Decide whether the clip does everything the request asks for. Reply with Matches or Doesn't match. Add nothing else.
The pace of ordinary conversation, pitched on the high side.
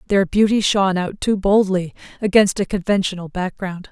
Matches